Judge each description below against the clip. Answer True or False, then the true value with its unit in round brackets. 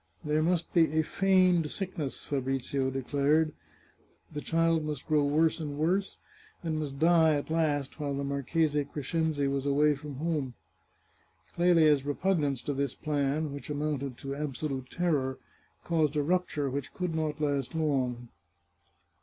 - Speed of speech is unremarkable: True (145 wpm)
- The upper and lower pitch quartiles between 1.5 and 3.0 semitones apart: True (2.5 semitones)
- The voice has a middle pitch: True (150 Hz)